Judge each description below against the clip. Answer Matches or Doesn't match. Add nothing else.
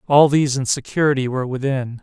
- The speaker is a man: Matches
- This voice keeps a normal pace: Matches